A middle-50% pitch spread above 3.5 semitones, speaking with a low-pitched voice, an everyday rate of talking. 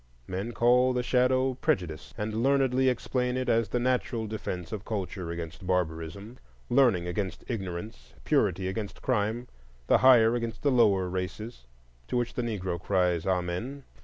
Yes: average, 5.3 semitones; low, 110 Hz; average, 150 wpm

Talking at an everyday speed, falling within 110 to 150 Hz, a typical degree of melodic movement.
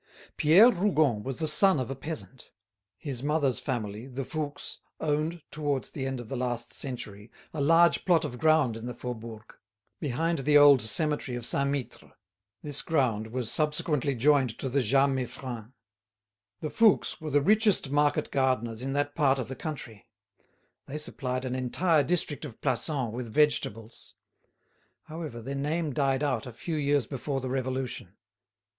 Yes: average, 165 wpm; low, 135 Hz; average, 3.4 semitones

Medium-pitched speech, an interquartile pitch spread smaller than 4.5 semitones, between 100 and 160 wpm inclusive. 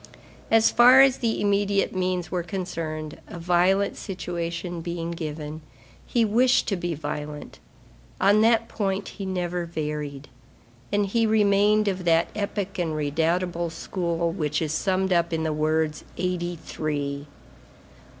Yes: medium, 175 Hz; average, 3.9 semitones; average, 140 wpm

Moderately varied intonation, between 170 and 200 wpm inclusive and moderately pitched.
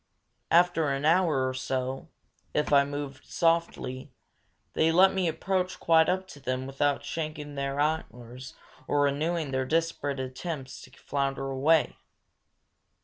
No: average, 3.5 semitones; slow, 135 wpm; medium, 145 Hz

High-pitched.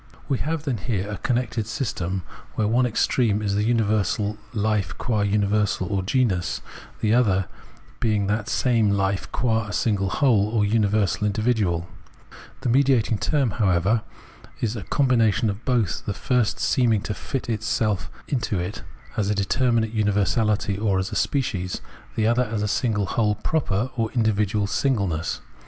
No: low, 105 Hz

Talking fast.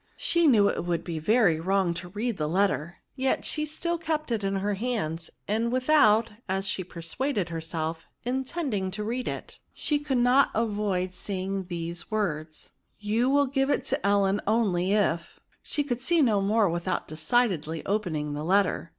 No: average, 175 wpm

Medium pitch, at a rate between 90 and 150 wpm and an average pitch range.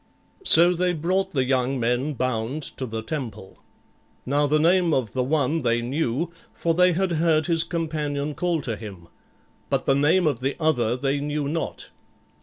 No: medium, 145 Hz; average, 175 wpm; average, 4.6 semitones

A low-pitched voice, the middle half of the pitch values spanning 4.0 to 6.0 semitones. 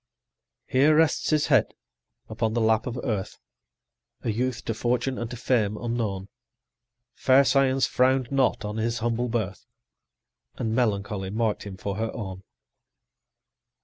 No: low, 115 Hz; average, 3.2 semitones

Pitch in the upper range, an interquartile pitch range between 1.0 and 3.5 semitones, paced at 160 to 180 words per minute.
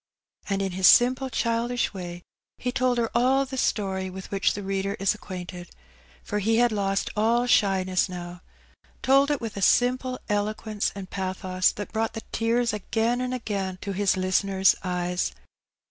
No: high, 205 Hz; average, 3.9 semitones; average, 170 wpm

